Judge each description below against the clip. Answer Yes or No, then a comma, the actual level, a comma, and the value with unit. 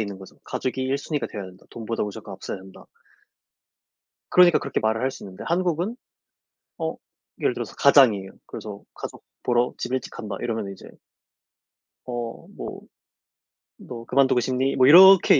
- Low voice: Yes, low, 120 Hz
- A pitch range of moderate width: Yes, average, 4.9 semitones